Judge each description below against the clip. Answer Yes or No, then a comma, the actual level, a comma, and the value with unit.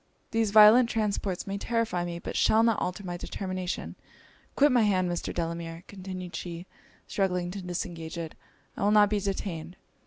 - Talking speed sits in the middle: Yes, average, 165 wpm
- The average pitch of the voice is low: No, medium, 185 Hz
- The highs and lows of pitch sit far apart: No, average, 3.2 semitones